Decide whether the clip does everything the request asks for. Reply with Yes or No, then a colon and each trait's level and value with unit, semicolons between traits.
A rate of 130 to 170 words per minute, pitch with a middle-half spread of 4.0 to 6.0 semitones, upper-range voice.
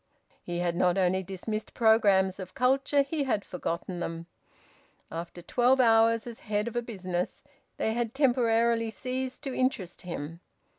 Yes: average, 150 wpm; average, 5.2 semitones; high, 220 Hz